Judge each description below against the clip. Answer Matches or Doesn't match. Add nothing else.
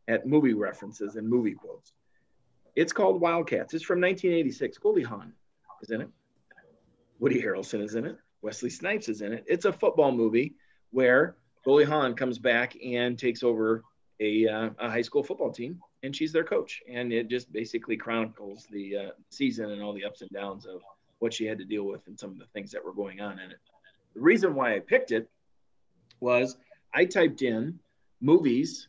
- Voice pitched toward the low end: Matches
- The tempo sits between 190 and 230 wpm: Matches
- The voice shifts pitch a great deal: Matches